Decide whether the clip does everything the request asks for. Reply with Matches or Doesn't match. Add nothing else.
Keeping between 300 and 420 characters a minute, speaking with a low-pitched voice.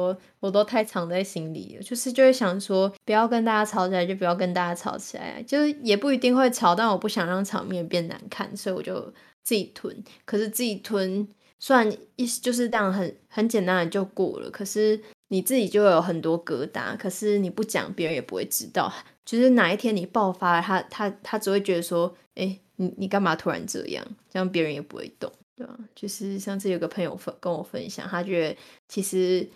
Doesn't match